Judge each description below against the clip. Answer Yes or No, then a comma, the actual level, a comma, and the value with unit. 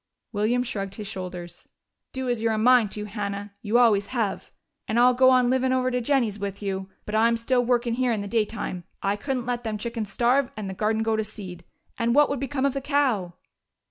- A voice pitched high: Yes, high, 230 Hz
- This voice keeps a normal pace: No, fast, 220 wpm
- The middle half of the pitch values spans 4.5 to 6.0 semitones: No, average, 3.5 semitones